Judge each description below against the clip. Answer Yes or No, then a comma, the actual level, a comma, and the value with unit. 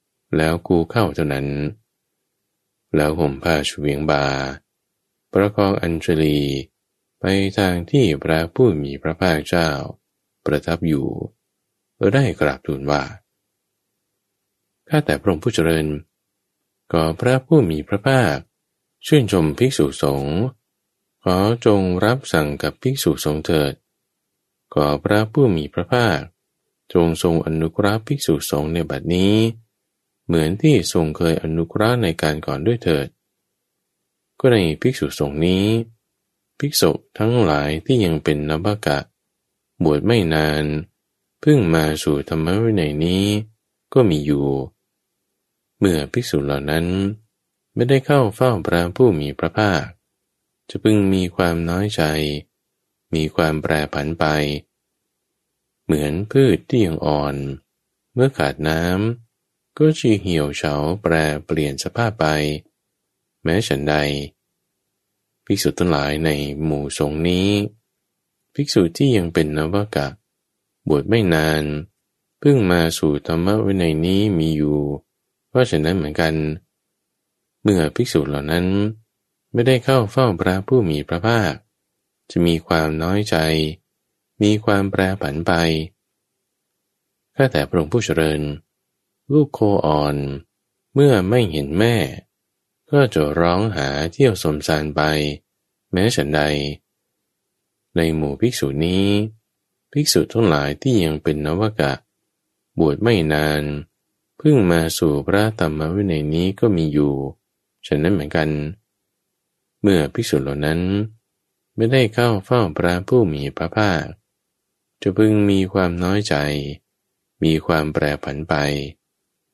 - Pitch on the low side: Yes, very low, 85 Hz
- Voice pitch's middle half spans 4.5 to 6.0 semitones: Yes, wide, 5.6 semitones